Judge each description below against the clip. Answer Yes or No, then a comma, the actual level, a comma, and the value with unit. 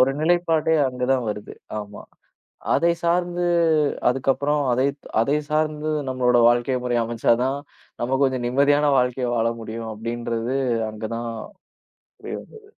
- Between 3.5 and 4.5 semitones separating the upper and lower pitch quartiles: Yes, average, 4.0 semitones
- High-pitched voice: No, low, 130 Hz